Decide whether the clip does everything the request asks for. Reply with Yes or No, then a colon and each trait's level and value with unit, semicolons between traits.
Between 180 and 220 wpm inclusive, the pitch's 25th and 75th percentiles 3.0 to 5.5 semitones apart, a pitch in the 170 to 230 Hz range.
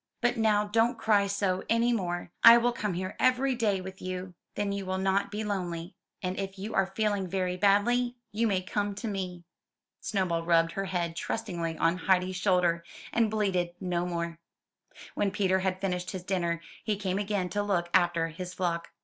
No: average, 190 wpm; narrow, 2.5 semitones; high, 190 Hz